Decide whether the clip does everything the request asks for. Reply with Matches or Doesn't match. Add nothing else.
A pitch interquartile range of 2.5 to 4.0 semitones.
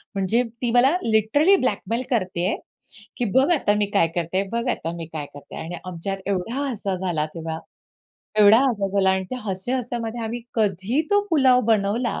Doesn't match